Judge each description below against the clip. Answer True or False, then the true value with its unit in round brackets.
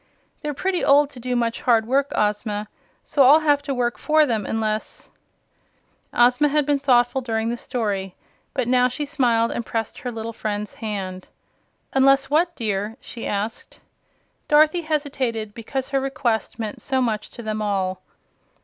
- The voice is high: True (240 Hz)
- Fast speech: False (165 wpm)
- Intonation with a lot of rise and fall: False (4.2 semitones)